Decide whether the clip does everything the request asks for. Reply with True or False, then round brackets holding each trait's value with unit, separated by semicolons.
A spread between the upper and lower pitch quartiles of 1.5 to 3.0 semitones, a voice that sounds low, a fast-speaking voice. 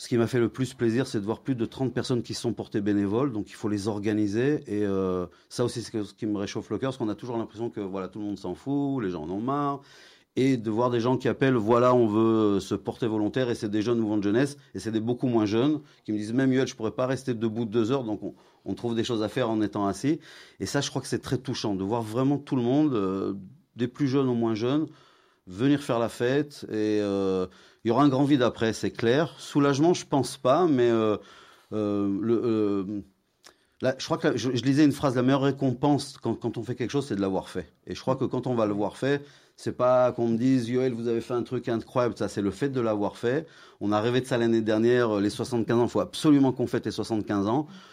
False (3.6 semitones; 115 Hz; 270 wpm)